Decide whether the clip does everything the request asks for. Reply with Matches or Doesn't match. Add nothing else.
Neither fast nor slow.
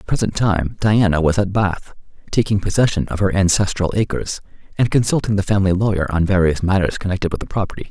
Matches